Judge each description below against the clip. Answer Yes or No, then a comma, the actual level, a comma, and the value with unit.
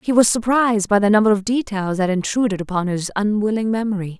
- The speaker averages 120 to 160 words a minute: No, average, 200 wpm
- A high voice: Yes, high, 210 Hz